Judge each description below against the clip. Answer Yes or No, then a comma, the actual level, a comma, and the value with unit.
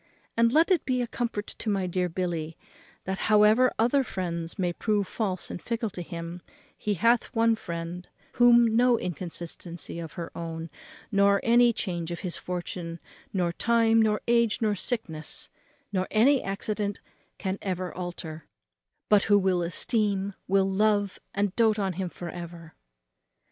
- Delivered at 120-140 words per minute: No, average, 155 wpm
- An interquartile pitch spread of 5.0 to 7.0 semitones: No, average, 4.3 semitones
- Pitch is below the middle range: No, high, 195 Hz